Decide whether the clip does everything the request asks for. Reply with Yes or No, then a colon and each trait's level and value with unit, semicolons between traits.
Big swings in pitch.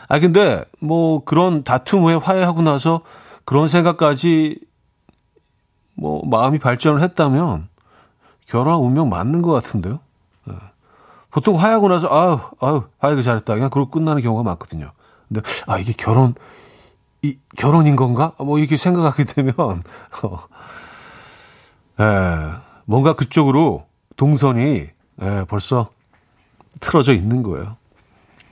Yes: wide, 6.2 semitones